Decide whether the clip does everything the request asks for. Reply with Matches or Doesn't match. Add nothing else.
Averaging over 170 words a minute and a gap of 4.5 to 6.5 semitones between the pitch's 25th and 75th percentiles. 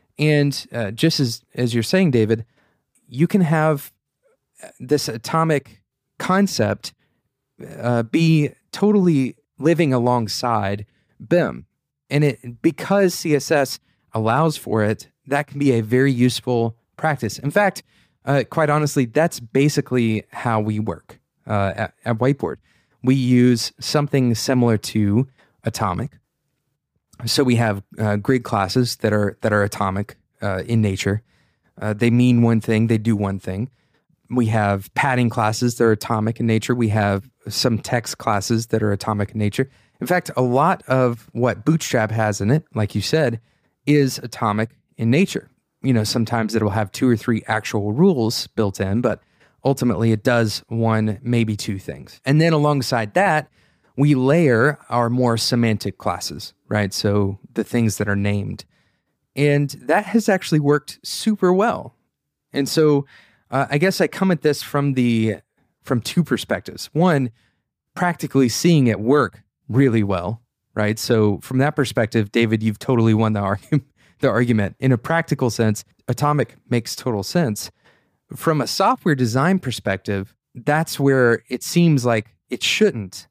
Doesn't match